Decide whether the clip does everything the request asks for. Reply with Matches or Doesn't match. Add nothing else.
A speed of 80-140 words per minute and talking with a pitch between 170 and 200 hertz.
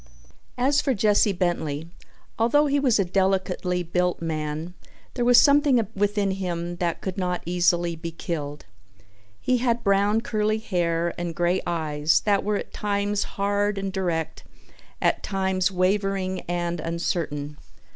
Matches